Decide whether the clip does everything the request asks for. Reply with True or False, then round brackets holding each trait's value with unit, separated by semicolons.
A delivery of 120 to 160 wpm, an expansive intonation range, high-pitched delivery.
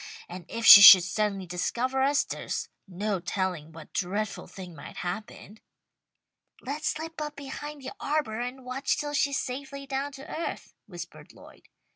True (155 wpm; 6.7 semitones; 245 Hz)